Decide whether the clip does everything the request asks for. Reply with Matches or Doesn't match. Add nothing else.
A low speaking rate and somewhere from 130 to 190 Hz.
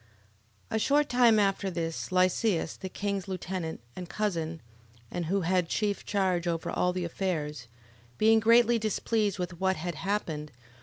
Doesn't match